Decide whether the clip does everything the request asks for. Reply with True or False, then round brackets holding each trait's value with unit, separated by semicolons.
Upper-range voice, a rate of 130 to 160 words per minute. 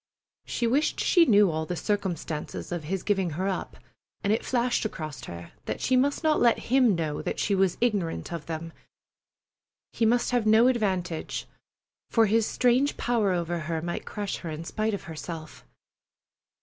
False (195 Hz; 175 wpm)